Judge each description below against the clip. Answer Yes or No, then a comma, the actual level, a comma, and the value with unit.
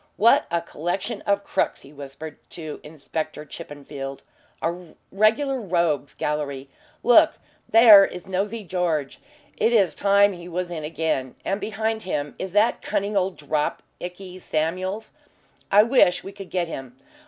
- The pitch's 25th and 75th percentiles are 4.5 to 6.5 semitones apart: Yes, average, 4.8 semitones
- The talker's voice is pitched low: No, medium, 180 Hz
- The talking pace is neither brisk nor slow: Yes, average, 145 wpm